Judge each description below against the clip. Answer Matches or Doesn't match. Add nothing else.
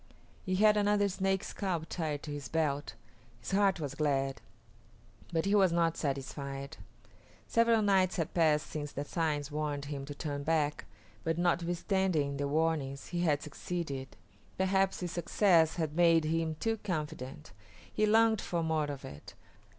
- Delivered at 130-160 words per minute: Matches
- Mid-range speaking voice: Matches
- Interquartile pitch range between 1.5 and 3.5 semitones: Doesn't match